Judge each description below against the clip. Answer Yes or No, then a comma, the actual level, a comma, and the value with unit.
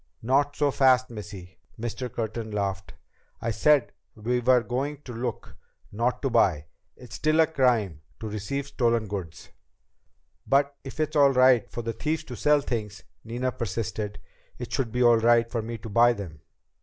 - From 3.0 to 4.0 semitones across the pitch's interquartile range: Yes, average, 3.6 semitones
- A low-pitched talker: Yes, low, 120 Hz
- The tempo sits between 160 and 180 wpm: Yes, average, 170 wpm